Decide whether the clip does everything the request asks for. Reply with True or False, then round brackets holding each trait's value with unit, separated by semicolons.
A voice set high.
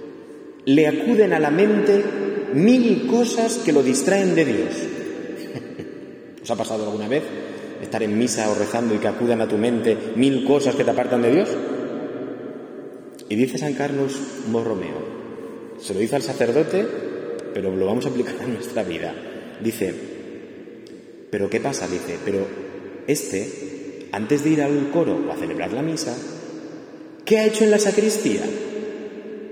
False (140 Hz)